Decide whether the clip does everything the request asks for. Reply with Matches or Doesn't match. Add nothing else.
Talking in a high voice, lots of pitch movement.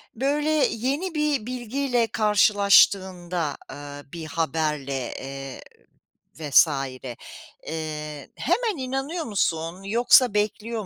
Matches